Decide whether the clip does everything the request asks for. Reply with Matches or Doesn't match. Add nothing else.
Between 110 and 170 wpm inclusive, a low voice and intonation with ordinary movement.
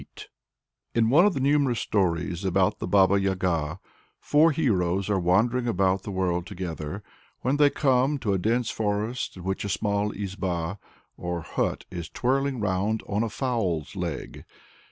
Matches